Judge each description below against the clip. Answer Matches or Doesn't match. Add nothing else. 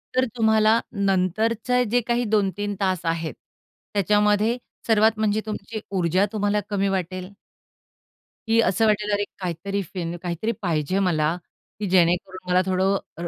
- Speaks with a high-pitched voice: Matches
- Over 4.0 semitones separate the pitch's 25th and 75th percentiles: Doesn't match